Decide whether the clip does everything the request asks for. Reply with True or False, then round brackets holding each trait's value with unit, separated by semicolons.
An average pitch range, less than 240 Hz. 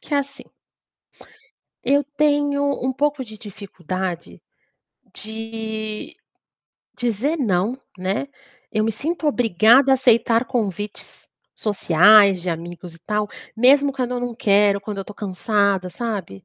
True (4.7 semitones; 220 Hz)